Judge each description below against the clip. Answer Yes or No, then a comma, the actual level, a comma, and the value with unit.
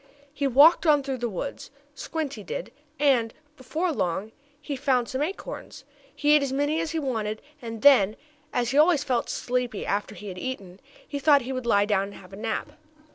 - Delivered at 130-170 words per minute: No, average, 200 wpm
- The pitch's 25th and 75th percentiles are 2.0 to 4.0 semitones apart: No, average, 5.2 semitones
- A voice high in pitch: Yes, very high, 255 Hz